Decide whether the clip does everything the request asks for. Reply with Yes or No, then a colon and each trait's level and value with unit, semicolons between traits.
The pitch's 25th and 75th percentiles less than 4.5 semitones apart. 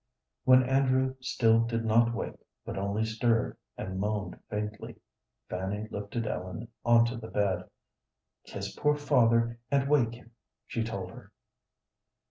Yes: average, 2.7 semitones